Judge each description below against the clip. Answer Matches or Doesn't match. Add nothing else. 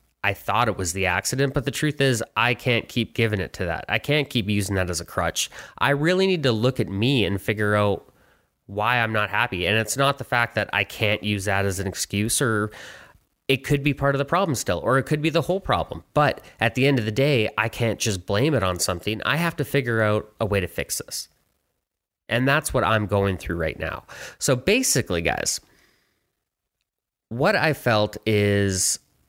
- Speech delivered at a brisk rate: Matches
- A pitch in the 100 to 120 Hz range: Matches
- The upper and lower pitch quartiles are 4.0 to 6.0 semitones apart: Matches